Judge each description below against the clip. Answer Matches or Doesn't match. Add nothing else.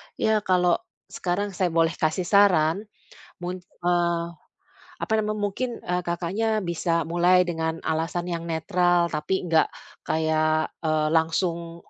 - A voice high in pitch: Doesn't match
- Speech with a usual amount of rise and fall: Doesn't match